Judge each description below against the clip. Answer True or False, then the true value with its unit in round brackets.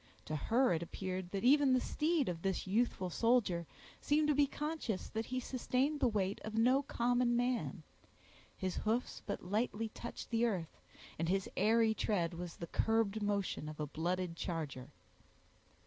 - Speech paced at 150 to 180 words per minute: True (165 wpm)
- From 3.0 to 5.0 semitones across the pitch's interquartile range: False (5.4 semitones)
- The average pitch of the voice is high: True (220 Hz)